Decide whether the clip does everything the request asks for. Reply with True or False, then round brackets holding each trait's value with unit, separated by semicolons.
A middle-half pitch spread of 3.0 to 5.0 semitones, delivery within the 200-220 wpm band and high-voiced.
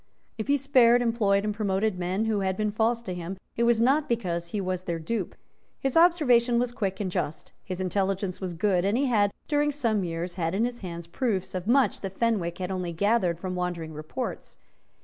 True (4.5 semitones; 205 wpm; 200 Hz)